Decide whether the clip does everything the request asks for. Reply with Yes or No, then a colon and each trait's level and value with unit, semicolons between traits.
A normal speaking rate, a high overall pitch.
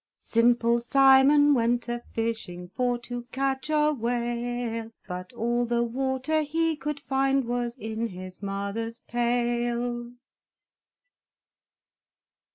No: slow, 105 wpm; high, 240 Hz